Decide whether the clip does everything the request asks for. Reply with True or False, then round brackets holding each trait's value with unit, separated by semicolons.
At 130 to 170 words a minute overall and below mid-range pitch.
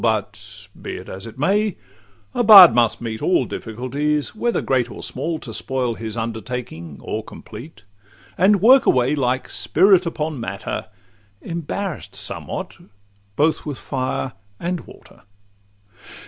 True (135 wpm; 130 Hz)